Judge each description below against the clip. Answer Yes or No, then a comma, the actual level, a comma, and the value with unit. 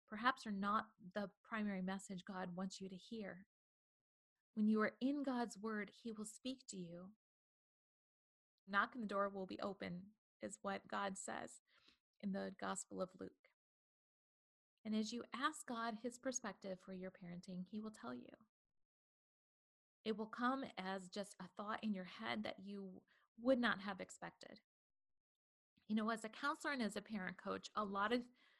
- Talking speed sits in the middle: Yes, average, 170 wpm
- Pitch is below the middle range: No, high, 210 Hz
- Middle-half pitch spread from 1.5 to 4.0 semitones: Yes, average, 3.3 semitones